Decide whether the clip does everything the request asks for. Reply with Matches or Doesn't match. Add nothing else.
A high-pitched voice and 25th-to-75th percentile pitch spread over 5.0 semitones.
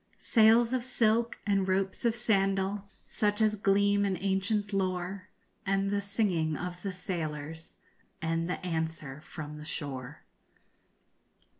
Doesn't match